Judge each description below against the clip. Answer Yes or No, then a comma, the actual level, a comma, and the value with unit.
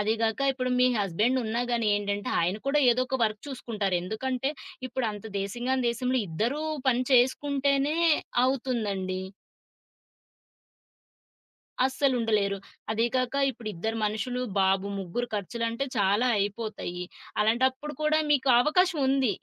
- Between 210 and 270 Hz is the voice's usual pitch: Yes, high, 235 Hz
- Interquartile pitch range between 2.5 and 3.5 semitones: No, average, 4.1 semitones